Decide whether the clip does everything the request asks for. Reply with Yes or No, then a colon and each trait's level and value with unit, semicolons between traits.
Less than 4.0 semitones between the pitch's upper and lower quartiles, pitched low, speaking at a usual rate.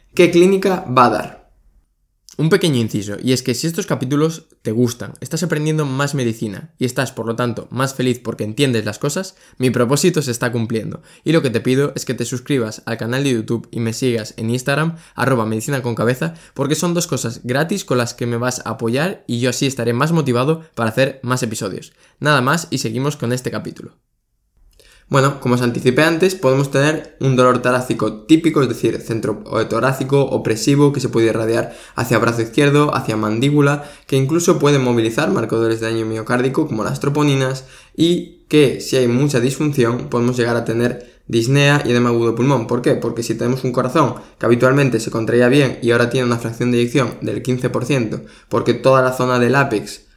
No: average, 3.6 semitones; low, 125 Hz; fast, 195 wpm